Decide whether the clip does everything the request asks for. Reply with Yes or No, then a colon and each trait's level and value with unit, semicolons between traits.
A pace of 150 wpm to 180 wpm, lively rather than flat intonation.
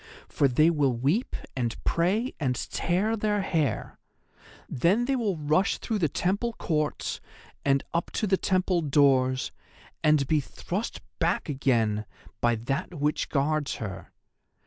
No: average, 140 wpm; wide, 5.8 semitones